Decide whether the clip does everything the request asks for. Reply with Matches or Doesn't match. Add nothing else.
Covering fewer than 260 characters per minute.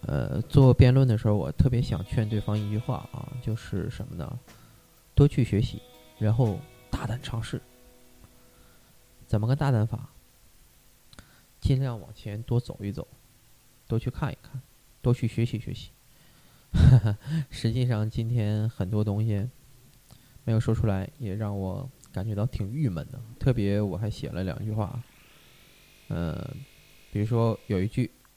Matches